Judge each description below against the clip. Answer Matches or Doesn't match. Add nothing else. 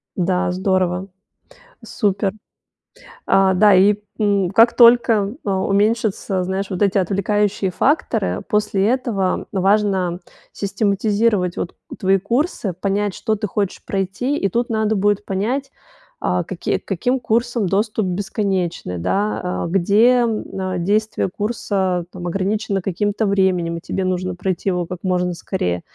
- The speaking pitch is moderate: Doesn't match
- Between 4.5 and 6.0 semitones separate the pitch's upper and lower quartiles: Doesn't match